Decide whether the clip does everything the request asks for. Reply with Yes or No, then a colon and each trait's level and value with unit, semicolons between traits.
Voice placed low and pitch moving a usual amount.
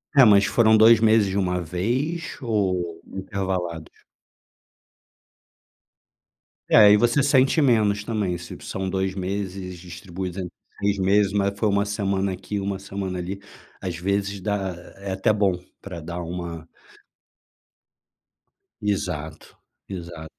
No: very low, 95 Hz; narrow, 2.3 semitones